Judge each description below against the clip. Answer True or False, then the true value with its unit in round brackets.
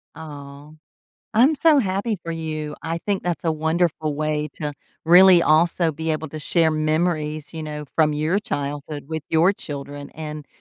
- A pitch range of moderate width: False (2.2 semitones)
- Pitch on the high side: False (155 Hz)